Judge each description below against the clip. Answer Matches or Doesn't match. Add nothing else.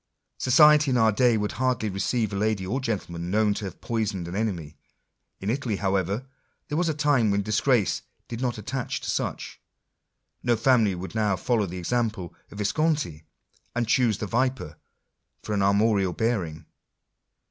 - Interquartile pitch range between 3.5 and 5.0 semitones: Matches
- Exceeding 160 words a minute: Matches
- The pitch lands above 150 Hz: Doesn't match